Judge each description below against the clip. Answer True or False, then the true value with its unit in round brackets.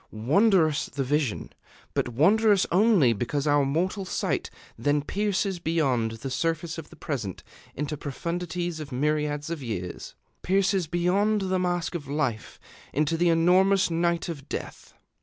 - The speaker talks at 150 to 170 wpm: False (140 wpm)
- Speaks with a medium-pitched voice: True (165 Hz)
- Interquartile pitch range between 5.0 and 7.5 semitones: False (4.1 semitones)